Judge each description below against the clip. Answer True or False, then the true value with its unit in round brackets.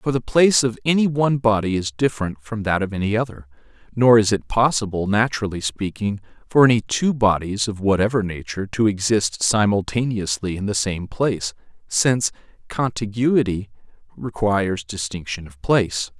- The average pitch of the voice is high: False (105 Hz)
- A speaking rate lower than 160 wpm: True (150 wpm)